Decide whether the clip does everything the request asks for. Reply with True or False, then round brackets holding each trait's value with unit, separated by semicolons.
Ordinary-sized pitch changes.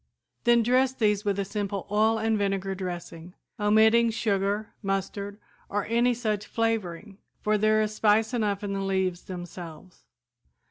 False (2.2 semitones)